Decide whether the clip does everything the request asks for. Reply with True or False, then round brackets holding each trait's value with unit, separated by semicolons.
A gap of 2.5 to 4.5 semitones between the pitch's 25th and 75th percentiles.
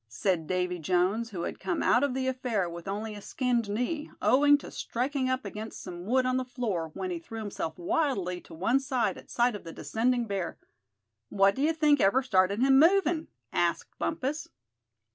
False (5.6 semitones)